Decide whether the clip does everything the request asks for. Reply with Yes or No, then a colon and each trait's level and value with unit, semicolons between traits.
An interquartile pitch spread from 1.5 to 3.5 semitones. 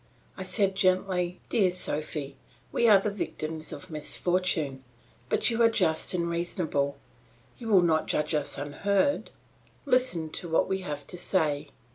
No: average, 4.0 semitones